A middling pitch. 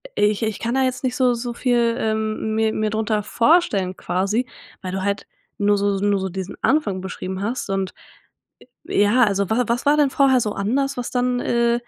No: high, 220 Hz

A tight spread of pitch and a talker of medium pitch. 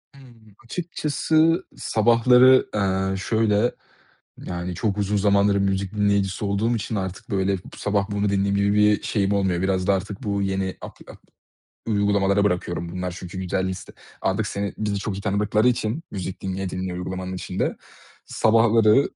No: narrow, 2.1 semitones; low, 100 Hz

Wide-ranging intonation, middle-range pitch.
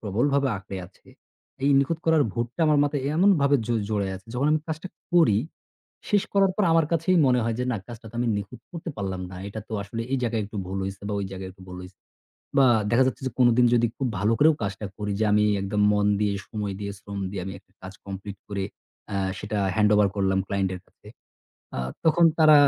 No: wide, 6.1 semitones; low, 110 Hz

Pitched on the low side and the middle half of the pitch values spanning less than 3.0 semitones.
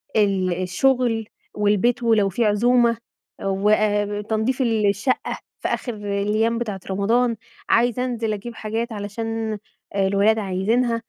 No: high, 220 Hz; narrow, 2.5 semitones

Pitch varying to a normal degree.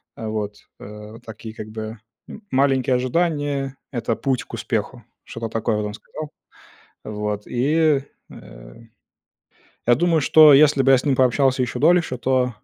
Yes: average, 4.3 semitones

